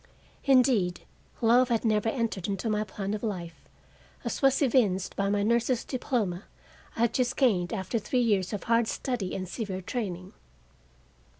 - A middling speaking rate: Yes, average, 160 wpm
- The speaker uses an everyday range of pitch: Yes, average, 4.0 semitones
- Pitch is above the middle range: Yes, high, 215 Hz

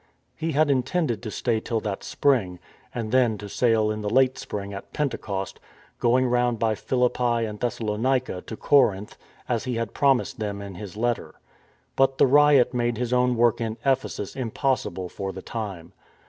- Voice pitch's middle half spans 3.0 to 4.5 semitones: Yes, average, 3.4 semitones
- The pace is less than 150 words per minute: No, average, 175 wpm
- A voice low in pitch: Yes, low, 120 Hz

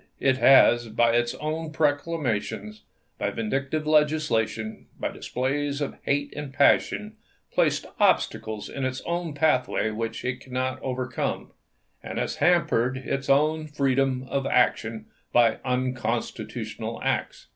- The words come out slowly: Yes, slow, 120 wpm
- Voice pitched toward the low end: Yes, low, 130 Hz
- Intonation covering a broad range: No, average, 3.4 semitones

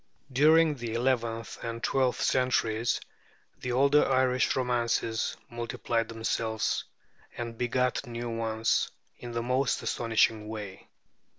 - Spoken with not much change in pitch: Yes, narrow, 1.9 semitones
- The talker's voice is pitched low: Yes, low, 120 Hz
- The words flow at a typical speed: No, slow, 110 wpm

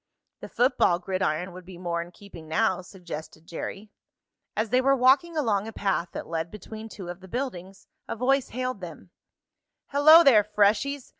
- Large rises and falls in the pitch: Yes, wide, 6.1 semitones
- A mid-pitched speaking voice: No, high, 200 Hz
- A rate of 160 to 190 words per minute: Yes, average, 170 wpm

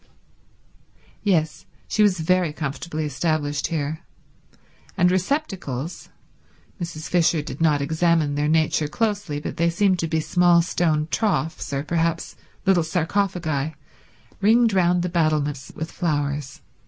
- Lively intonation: No, average, 3.0 semitones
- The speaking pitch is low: No, medium, 165 Hz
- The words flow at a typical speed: No, slow, 120 wpm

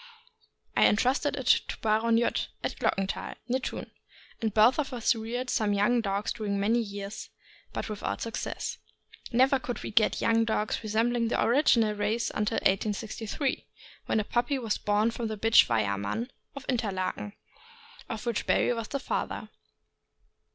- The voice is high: Yes, high, 225 Hz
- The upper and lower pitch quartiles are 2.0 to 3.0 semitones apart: Yes, narrow, 2.5 semitones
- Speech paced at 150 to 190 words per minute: Yes, average, 155 wpm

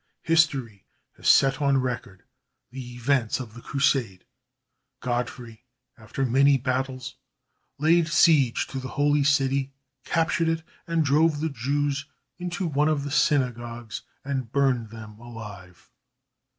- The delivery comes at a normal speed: No, slow, 125 wpm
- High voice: No, low, 135 Hz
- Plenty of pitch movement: No, average, 3.4 semitones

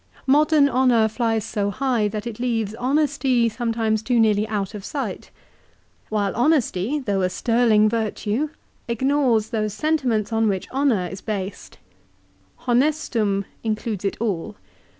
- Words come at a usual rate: No, slow, 130 wpm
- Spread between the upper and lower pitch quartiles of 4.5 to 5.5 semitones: No, average, 3.5 semitones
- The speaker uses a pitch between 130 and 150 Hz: No, high, 225 Hz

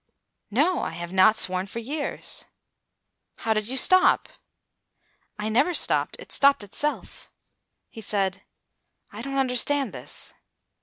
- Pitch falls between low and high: No, high, 230 Hz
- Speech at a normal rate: No, slow, 130 wpm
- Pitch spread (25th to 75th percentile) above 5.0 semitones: Yes, wide, 5.6 semitones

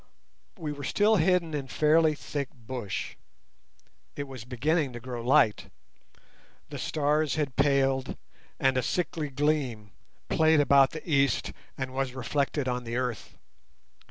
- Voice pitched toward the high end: No, medium, 140 Hz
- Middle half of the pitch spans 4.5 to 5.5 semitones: No, average, 3.0 semitones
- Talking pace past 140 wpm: No, slow, 135 wpm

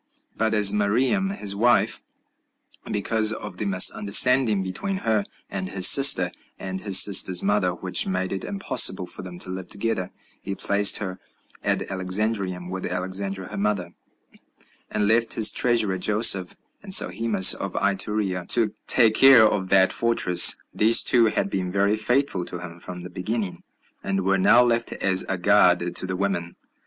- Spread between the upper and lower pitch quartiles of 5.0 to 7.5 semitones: No, average, 3.1 semitones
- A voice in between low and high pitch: No, low, 100 Hz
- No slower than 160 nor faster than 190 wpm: Yes, average, 165 wpm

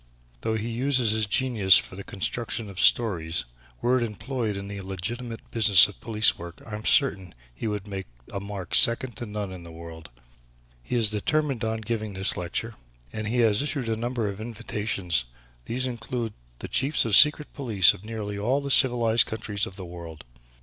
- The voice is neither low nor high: No, low, 110 Hz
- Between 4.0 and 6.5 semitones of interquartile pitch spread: No, average, 3.5 semitones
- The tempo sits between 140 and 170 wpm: No, average, 190 wpm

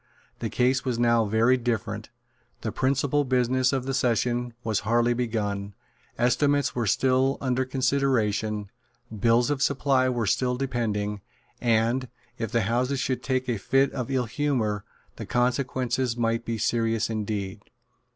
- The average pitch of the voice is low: Yes, low, 120 Hz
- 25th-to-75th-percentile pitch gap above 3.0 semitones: No, narrow, 2.6 semitones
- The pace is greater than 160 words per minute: No, average, 140 wpm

